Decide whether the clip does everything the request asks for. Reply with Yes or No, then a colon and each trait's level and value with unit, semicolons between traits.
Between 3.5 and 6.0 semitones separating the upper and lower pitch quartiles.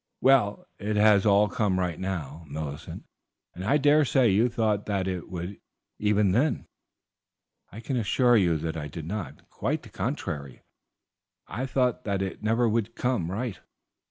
Yes: average, 4.4 semitones